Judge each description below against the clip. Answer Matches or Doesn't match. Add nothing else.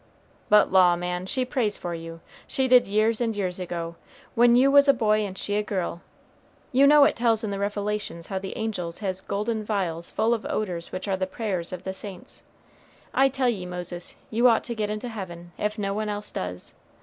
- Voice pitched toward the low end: Doesn't match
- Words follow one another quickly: Matches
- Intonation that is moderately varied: Matches